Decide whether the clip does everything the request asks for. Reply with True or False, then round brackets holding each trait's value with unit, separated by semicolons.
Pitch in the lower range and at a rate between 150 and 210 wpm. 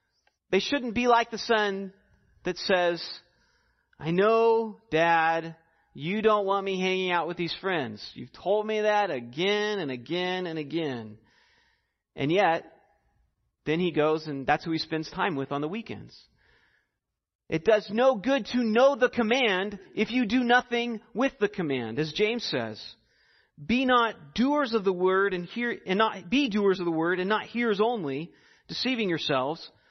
False (195 Hz; 165 wpm)